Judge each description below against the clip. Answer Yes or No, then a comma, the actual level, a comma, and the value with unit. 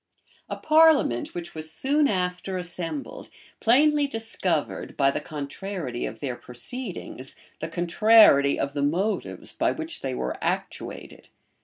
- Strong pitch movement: Yes, wide, 8.6 semitones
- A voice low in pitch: No, medium, 180 Hz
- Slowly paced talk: Yes, slow, 130 wpm